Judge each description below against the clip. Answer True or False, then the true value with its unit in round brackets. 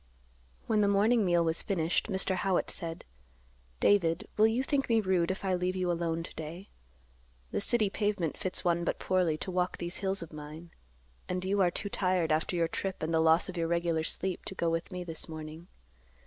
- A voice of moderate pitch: True (180 Hz)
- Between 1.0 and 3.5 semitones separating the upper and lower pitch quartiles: True (2.6 semitones)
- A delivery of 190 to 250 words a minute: True (205 wpm)